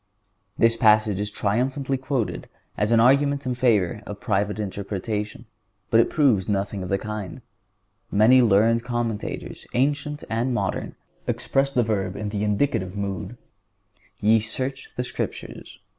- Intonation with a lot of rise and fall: No, average, 3.6 semitones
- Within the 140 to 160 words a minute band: Yes, average, 145 wpm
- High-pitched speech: No, low, 110 Hz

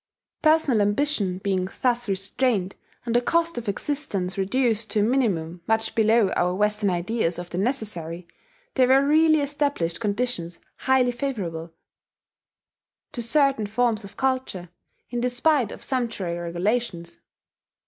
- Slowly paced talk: Yes, slow, 130 wpm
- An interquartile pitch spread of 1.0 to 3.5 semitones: No, wide, 5.6 semitones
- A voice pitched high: Yes, high, 220 Hz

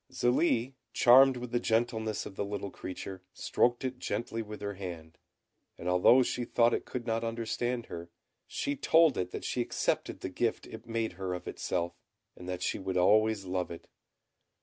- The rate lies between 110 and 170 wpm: No, average, 180 wpm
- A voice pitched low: Yes, low, 110 Hz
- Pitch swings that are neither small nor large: Yes, average, 4.7 semitones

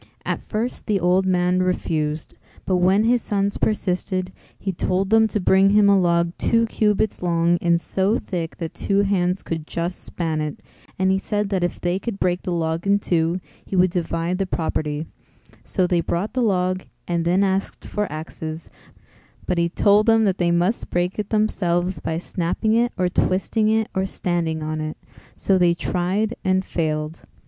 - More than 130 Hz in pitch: Yes, medium, 185 Hz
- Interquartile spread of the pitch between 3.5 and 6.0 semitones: No, average, 2.7 semitones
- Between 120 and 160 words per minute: No, average, 185 wpm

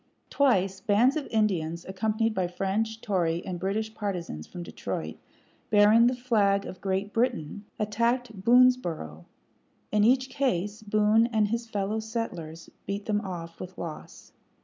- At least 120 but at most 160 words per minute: Yes, average, 140 wpm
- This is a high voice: Yes, high, 210 Hz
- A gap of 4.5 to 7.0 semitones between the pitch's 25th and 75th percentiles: No, average, 3.4 semitones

